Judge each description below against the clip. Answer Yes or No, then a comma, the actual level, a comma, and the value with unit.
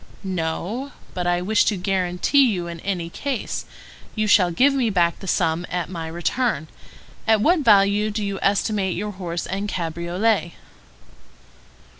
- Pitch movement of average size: Yes, average, 3.7 semitones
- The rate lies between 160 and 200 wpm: No, average, 150 wpm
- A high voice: Yes, high, 195 Hz